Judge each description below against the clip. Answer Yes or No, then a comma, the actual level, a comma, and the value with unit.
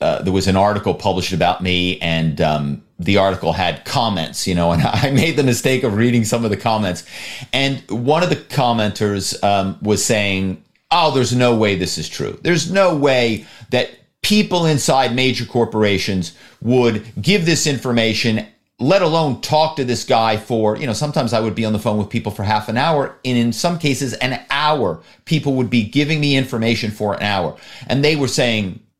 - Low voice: Yes, low, 115 Hz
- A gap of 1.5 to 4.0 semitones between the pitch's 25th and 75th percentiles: No, average, 4.7 semitones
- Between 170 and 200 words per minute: Yes, average, 195 wpm